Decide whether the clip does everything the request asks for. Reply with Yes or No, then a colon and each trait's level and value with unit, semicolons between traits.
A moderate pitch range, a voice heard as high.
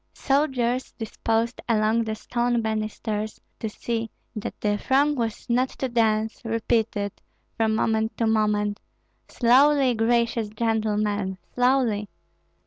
No: narrow, 2.0 semitones; high, 225 Hz